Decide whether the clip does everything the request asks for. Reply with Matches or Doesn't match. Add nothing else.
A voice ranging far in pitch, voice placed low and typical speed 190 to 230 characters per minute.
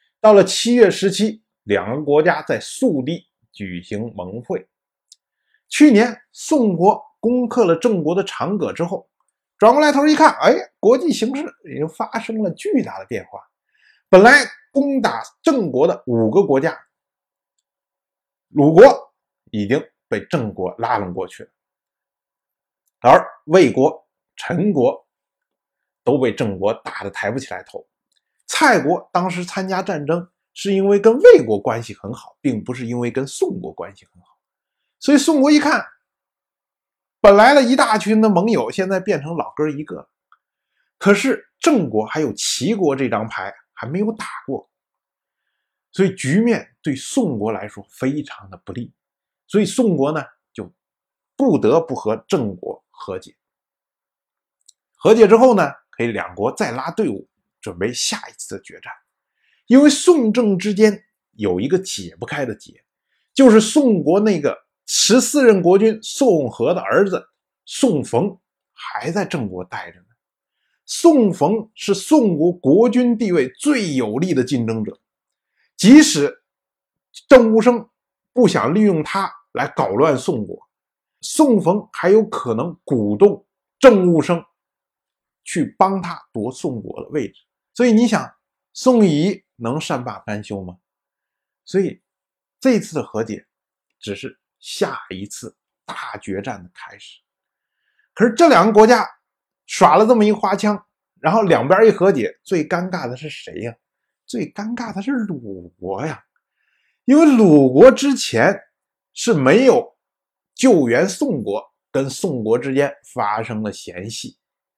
Doesn't match